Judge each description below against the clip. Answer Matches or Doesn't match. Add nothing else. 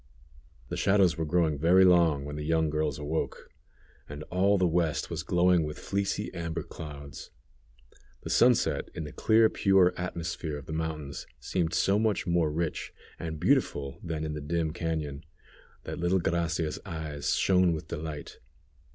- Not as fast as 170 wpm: Matches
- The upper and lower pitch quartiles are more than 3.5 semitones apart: Doesn't match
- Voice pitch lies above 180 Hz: Doesn't match